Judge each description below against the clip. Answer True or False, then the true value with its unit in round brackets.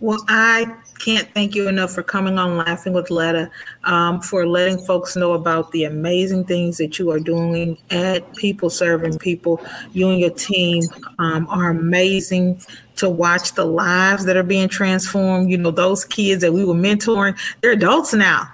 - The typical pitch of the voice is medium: True (180 Hz)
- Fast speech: False (180 wpm)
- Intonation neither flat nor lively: False (2.2 semitones)